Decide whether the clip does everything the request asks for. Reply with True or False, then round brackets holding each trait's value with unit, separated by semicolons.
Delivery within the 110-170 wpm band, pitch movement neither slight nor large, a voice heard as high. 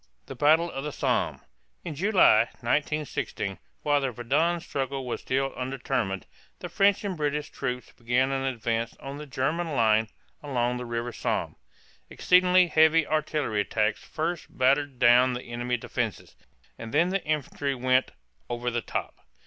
False (155 wpm; 4.2 semitones; 135 Hz)